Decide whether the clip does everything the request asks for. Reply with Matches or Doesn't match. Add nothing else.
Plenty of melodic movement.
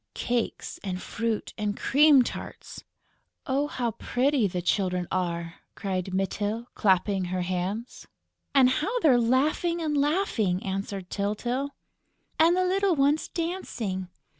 Matches